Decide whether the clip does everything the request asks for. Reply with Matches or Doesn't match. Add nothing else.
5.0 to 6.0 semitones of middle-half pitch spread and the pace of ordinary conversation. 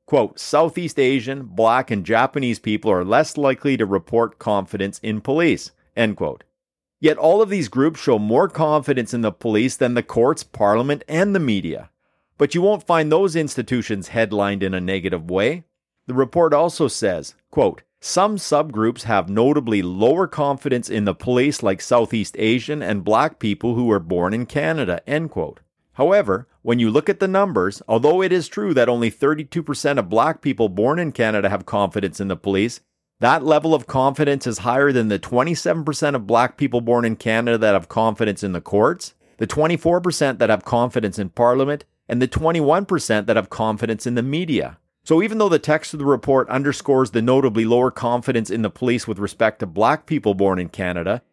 Matches